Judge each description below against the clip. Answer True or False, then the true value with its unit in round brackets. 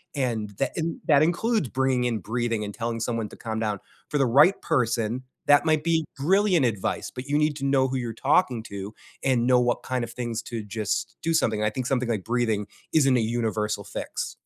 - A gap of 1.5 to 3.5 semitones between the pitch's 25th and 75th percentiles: False (4.2 semitones)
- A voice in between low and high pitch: False (125 Hz)